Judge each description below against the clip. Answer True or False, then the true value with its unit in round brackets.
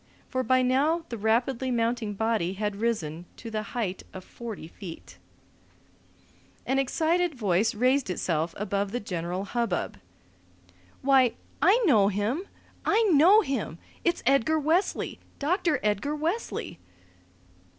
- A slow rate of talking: True (125 wpm)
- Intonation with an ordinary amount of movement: False (5.9 semitones)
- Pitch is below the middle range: False (235 Hz)